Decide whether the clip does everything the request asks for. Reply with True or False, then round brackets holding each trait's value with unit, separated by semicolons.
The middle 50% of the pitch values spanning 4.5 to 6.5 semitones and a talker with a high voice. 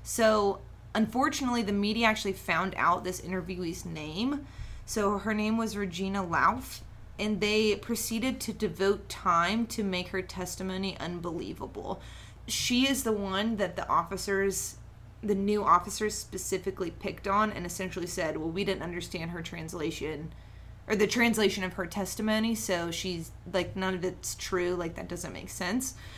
False (3.6 semitones; 195 Hz)